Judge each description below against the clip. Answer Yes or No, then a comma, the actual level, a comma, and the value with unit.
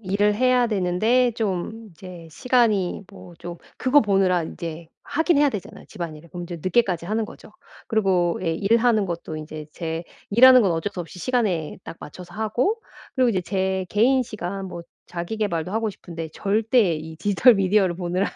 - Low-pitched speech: No, high, 195 Hz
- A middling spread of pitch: Yes, average, 4.5 semitones